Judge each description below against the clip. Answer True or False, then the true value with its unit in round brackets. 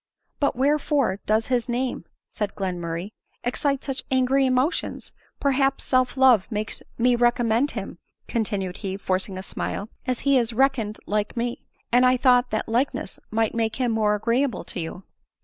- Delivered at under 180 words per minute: True (170 wpm)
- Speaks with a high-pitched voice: True (240 Hz)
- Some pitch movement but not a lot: True (3.7 semitones)